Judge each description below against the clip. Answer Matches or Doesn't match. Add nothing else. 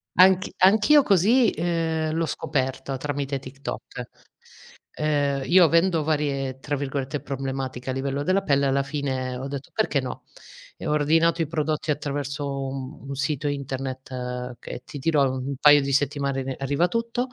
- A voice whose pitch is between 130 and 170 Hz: Matches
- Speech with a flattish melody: Doesn't match